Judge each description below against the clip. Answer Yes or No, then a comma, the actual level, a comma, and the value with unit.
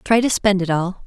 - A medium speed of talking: No, fast, 280 wpm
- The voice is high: Yes, high, 195 Hz